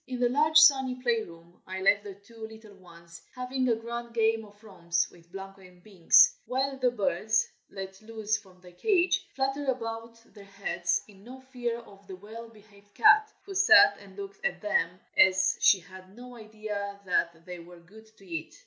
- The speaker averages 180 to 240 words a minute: Yes, average, 195 wpm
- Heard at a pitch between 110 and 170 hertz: No, high, 215 Hz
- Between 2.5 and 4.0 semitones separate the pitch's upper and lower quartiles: No, average, 4.7 semitones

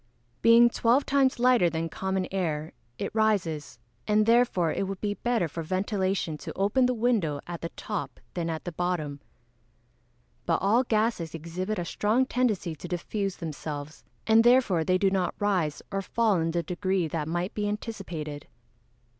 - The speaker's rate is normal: Yes, average, 170 wpm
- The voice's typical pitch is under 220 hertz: Yes, high, 190 Hz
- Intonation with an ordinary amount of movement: Yes, average, 4.7 semitones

